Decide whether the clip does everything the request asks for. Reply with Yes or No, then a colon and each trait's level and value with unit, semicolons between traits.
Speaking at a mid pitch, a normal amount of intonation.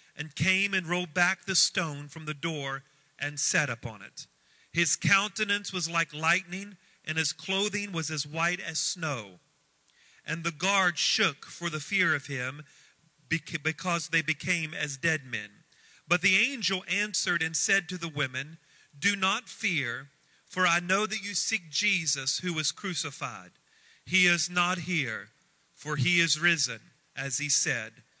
Yes: medium, 170 Hz; average, 4.2 semitones